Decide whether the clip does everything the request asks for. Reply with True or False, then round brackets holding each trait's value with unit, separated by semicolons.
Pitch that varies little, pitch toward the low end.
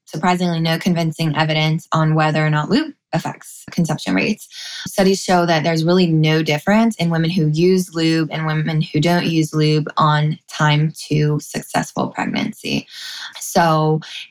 False (2.3 semitones; 160 Hz)